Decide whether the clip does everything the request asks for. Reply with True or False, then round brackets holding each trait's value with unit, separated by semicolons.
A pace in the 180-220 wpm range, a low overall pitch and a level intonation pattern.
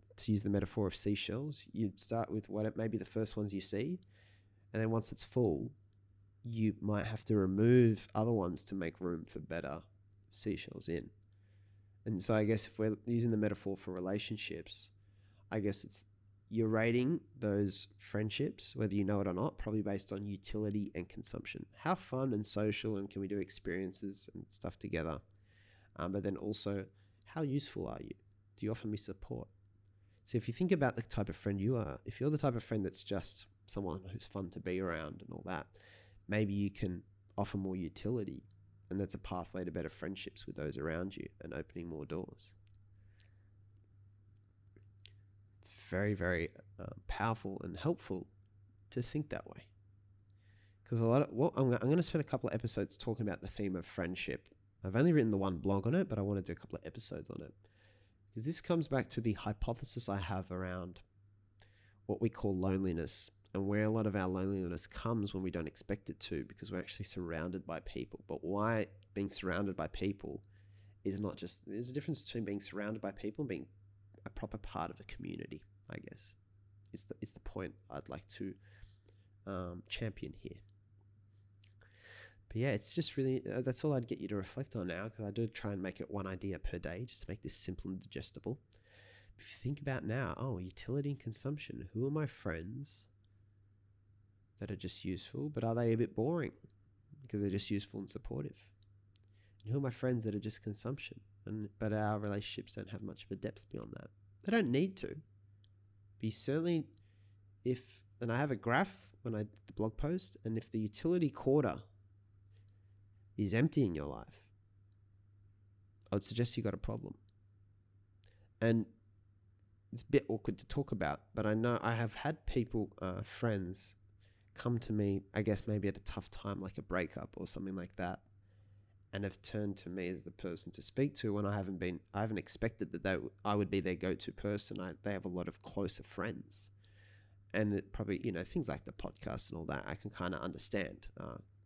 True (195 wpm; 100 Hz; 1.9 semitones)